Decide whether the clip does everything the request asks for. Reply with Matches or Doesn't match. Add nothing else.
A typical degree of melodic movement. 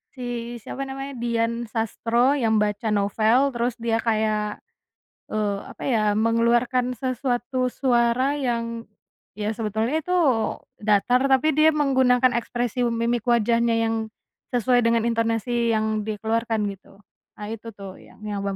Doesn't match